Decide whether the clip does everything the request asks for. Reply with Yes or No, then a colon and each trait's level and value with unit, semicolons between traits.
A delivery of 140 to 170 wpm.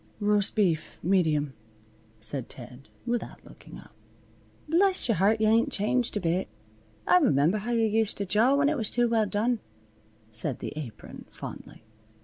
Yes: average, 160 wpm